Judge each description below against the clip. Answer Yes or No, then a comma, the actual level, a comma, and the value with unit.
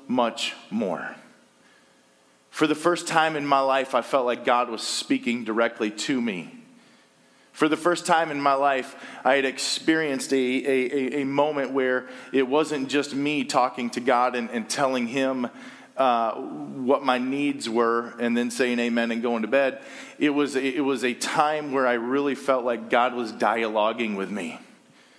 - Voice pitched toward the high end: No, low, 135 Hz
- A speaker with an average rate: Yes, average, 175 wpm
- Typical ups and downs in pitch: Yes, average, 3.1 semitones